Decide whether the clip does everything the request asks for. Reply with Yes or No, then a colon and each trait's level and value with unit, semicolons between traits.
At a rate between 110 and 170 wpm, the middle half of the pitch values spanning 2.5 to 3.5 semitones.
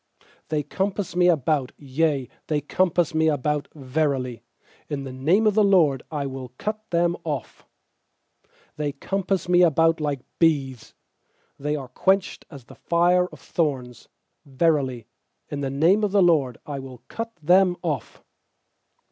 No: average, 150 wpm; average, 4.5 semitones